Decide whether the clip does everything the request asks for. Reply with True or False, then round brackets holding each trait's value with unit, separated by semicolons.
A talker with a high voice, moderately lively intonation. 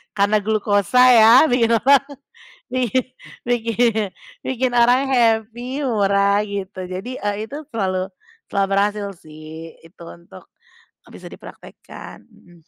True (215 Hz; 3.7 semitones)